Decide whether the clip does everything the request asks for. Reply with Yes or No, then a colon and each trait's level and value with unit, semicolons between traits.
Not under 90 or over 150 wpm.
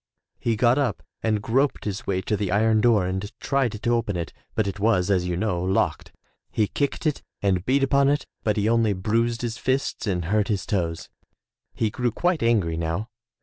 No: average, 200 wpm